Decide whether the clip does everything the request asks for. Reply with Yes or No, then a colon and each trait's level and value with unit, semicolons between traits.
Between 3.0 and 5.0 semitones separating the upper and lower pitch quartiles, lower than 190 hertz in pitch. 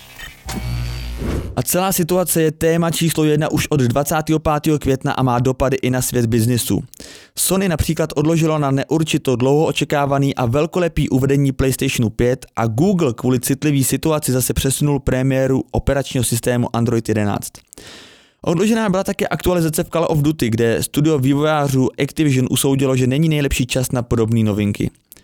Yes: average, 3.9 semitones; medium, 140 Hz